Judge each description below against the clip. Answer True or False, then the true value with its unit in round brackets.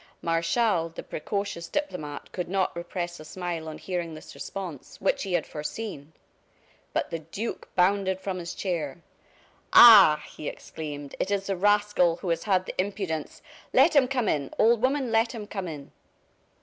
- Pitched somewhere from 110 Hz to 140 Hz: False (180 Hz)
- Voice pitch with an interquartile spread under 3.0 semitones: False (4.1 semitones)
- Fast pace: False (165 wpm)